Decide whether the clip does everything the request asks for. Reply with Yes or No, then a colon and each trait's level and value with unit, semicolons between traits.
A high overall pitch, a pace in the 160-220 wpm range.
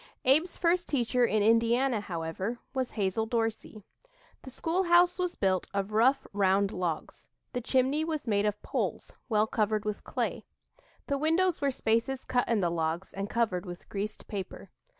Yes: high, 225 Hz; average, 165 wpm